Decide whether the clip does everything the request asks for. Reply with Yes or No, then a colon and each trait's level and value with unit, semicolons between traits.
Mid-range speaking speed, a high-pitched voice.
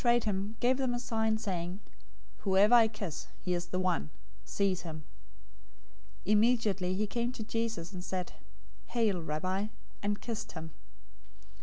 Yes: average, 170 wpm; high, 205 Hz